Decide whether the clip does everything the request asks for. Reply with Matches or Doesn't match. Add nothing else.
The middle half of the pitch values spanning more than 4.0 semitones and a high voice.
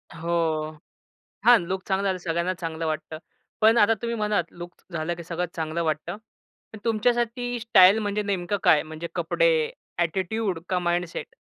Doesn't match